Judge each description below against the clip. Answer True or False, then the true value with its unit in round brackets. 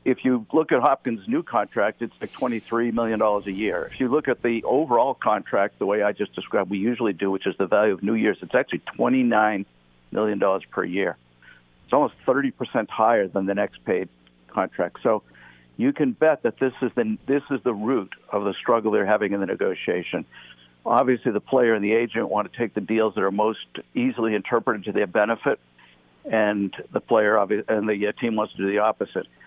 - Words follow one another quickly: True (210 wpm)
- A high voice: False (110 Hz)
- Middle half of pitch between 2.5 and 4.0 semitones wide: True (3.6 semitones)